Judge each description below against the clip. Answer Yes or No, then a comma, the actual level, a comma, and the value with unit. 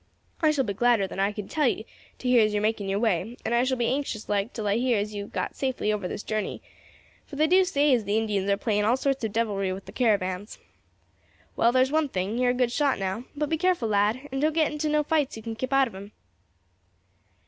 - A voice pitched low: No, high, 230 Hz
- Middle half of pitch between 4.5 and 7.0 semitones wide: Yes, average, 4.8 semitones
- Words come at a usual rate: No, fast, 260 wpm